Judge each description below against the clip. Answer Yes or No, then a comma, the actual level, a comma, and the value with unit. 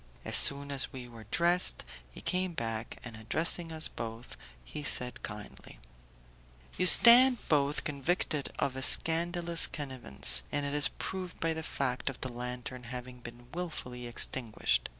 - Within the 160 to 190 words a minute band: No, average, 150 wpm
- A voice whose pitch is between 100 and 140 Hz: Yes, low, 135 Hz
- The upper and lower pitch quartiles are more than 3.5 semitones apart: Yes, average, 5.1 semitones